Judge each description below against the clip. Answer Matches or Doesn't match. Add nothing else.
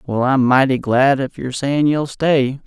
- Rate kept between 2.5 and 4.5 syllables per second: Matches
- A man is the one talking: Matches